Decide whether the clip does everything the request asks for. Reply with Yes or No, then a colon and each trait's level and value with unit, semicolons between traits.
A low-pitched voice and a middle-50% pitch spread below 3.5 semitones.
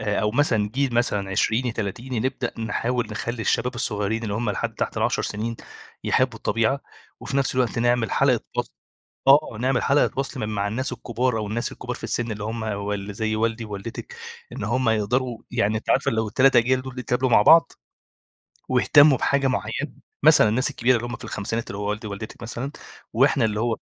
Yes: low, 115 Hz; average, 3.0 semitones